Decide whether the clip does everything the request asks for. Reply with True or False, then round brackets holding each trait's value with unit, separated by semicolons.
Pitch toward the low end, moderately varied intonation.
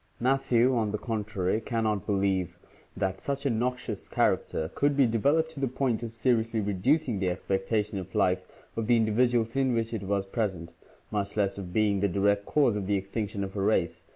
True (110 Hz; 3.5 semitones)